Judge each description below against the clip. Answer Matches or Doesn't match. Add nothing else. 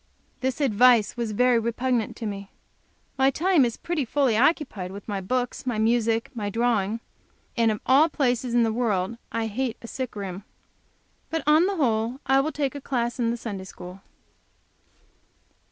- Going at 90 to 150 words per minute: Doesn't match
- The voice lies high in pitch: Matches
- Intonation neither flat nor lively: Matches